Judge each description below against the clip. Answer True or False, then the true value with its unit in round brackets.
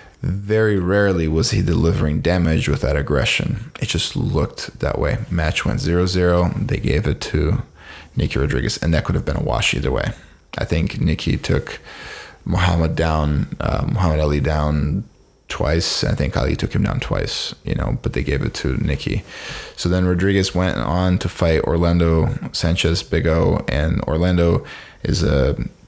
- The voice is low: True (85 Hz)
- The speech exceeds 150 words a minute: True (170 wpm)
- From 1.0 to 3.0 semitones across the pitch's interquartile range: True (2.7 semitones)